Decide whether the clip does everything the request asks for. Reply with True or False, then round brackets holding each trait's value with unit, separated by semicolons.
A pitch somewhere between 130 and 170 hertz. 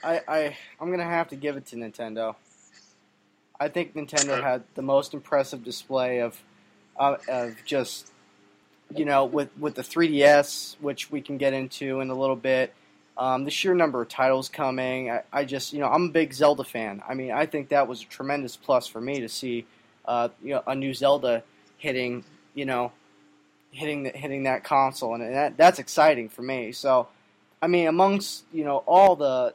True (135 Hz)